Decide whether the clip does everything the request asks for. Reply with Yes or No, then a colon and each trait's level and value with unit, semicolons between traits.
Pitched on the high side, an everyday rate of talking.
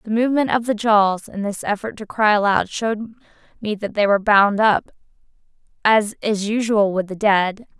Yes: high, 210 Hz; average, 185 wpm